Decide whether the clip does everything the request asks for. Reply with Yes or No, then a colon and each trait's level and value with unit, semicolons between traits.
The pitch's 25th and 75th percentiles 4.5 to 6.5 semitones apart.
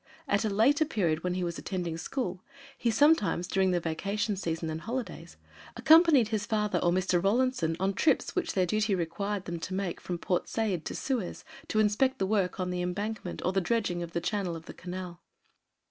No: average, 3.7 semitones